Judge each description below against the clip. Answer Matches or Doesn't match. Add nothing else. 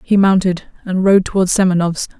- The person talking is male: Doesn't match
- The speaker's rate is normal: Matches